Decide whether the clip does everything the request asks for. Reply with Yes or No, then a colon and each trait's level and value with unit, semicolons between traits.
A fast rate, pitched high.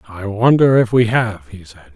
No: fast, 215 wpm; low, 105 Hz